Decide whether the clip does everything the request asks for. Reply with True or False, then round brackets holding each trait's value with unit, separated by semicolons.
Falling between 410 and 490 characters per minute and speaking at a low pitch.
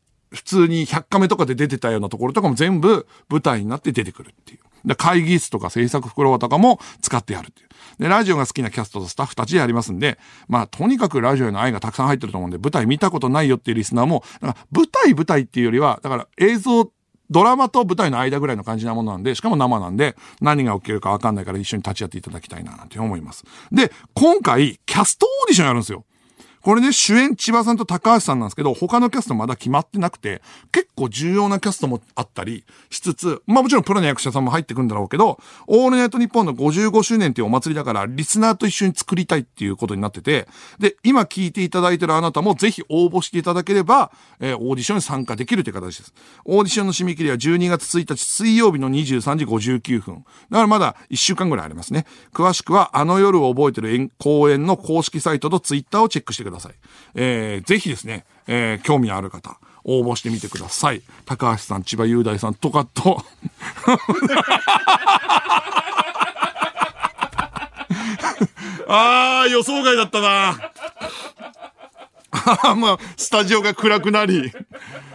False (425 characters per minute; 150 Hz)